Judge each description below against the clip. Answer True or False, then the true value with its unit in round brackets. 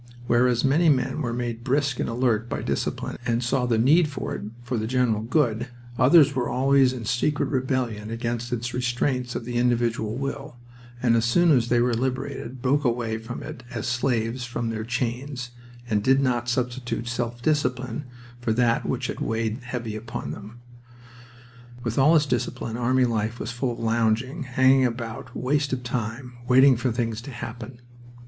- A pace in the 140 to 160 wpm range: False (175 wpm)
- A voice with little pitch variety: True (2.0 semitones)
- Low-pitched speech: True (120 Hz)